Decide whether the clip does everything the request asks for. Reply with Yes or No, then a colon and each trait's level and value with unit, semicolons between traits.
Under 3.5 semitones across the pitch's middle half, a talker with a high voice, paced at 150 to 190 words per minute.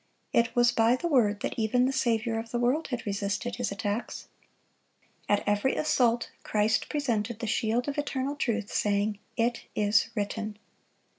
Yes: average, 2.8 semitones; high, 230 Hz; average, 160 wpm